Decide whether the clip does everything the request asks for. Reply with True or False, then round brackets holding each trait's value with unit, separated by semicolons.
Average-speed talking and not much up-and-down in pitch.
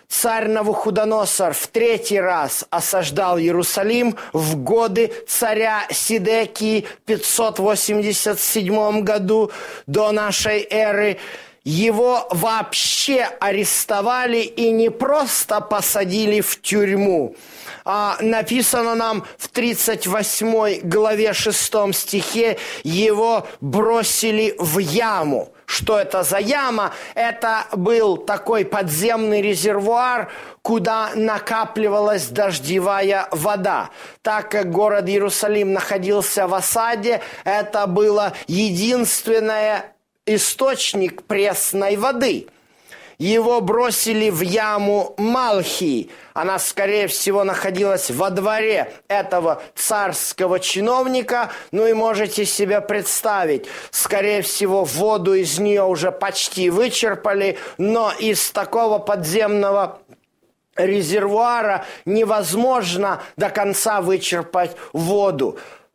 False (90 wpm; 2.1 semitones)